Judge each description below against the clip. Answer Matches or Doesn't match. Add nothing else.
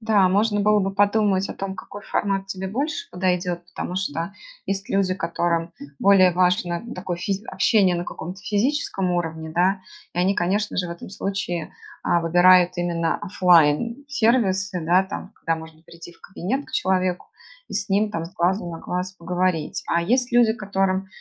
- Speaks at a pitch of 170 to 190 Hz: Matches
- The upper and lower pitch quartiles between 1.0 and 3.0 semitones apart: Matches